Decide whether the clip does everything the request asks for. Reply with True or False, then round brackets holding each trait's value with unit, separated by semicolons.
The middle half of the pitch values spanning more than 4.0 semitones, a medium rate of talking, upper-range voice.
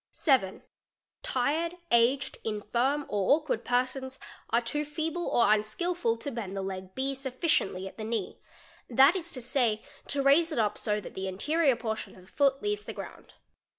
True (5.3 semitones; 180 wpm; 255 Hz)